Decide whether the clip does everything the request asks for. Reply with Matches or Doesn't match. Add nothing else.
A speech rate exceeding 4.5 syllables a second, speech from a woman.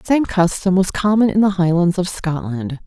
Matches